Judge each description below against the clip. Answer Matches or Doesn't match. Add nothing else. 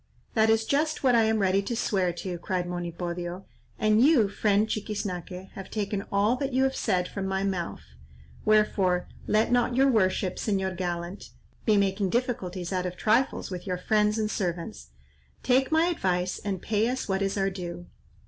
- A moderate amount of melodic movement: Matches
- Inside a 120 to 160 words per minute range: Doesn't match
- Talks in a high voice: Matches